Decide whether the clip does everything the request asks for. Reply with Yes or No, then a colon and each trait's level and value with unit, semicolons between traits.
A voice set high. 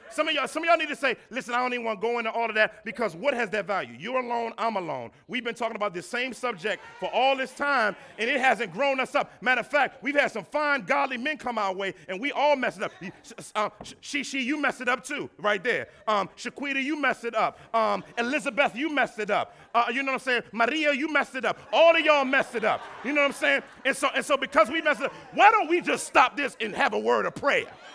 Yes: very high, 255 Hz